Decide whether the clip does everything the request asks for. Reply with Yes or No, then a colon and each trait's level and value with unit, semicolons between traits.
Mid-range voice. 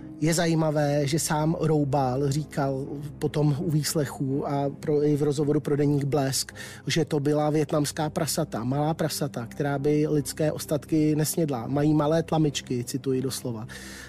Yes: medium, 150 Hz